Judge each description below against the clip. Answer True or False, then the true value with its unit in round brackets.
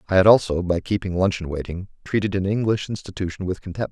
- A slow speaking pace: False (200 wpm)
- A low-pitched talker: True (95 Hz)